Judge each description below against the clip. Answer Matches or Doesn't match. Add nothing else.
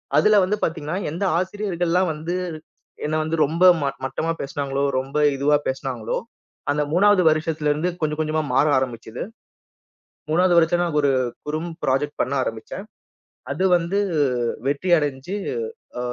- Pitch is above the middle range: Doesn't match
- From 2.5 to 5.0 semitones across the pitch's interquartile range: Matches